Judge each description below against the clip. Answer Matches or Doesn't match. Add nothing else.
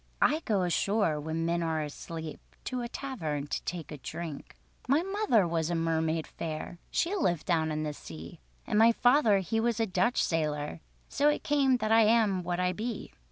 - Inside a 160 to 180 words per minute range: Doesn't match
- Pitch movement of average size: Doesn't match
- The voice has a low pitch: Doesn't match